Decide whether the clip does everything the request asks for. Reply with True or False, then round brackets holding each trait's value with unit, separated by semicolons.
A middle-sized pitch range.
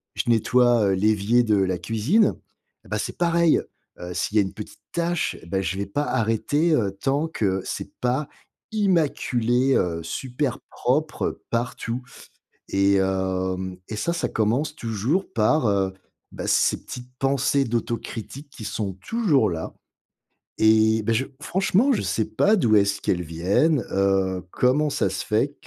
False (6.6 semitones)